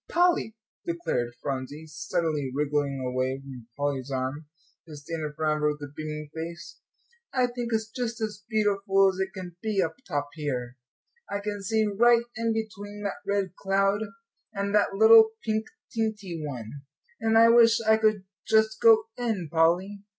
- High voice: Yes, high, 195 Hz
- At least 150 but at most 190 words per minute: Yes, average, 165 wpm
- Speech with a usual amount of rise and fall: No, wide, 6.6 semitones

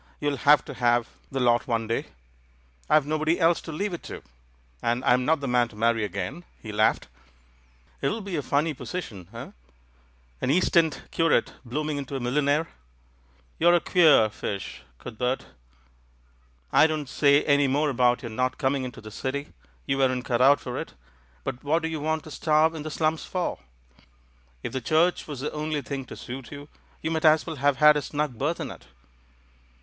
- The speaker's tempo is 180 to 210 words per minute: Yes, average, 200 wpm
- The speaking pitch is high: No, medium, 140 Hz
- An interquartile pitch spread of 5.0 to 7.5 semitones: No, average, 4.4 semitones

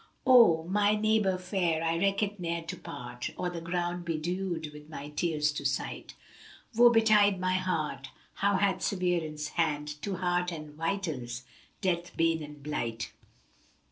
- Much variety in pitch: No, average, 3.8 semitones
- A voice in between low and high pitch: Yes, medium, 170 Hz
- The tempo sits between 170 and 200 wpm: No, average, 155 wpm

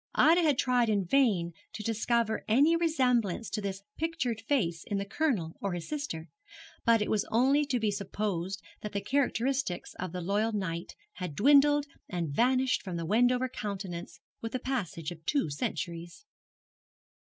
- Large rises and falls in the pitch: Yes, wide, 6.1 semitones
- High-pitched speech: Yes, high, 215 Hz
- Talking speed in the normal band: Yes, average, 165 wpm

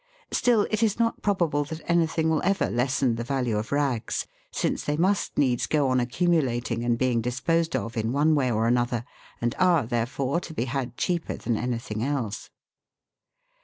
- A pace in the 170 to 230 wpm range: Yes, average, 180 wpm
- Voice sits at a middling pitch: No, low, 130 Hz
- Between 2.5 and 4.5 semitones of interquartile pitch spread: No, average, 5.3 semitones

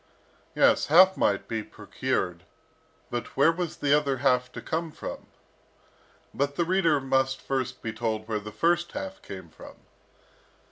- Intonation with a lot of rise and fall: Yes, wide, 6.6 semitones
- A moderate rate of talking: Yes, average, 150 wpm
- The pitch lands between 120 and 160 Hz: Yes, low, 135 Hz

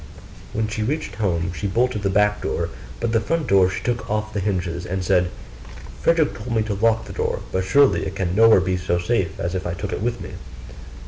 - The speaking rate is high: Yes, fast, 220 wpm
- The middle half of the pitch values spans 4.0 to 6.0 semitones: No, average, 3.5 semitones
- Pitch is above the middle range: No, low, 100 Hz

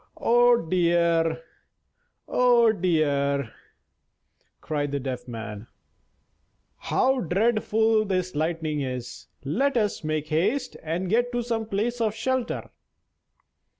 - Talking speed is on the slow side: Yes, slow, 105 wpm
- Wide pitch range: Yes, wide, 7.0 semitones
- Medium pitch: Yes, medium, 180 Hz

